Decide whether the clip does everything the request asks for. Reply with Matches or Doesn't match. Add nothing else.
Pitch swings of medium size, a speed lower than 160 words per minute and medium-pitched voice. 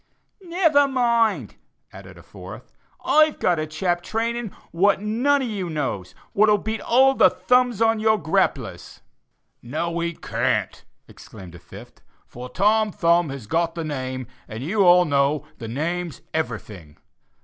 Doesn't match